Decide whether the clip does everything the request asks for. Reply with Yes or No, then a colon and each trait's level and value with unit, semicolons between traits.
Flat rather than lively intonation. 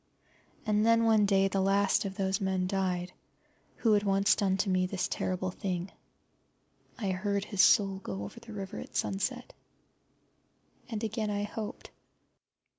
Yes: narrow, 1.9 semitones